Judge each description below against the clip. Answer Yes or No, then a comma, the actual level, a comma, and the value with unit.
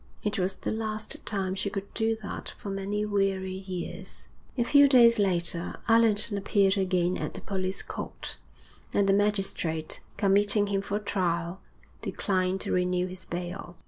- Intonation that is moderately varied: No, narrow, 2.0 semitones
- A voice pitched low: No, high, 195 Hz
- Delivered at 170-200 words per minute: No, average, 155 wpm